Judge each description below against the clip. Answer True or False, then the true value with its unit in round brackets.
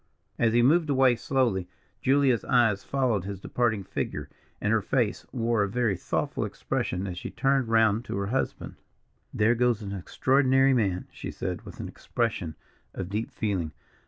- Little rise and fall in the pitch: False (4.6 semitones)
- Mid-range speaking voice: False (115 Hz)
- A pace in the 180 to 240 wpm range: False (165 wpm)